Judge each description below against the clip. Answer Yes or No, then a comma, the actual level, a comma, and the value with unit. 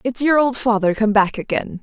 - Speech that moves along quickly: Yes, fast, 230 wpm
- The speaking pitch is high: Yes, high, 230 Hz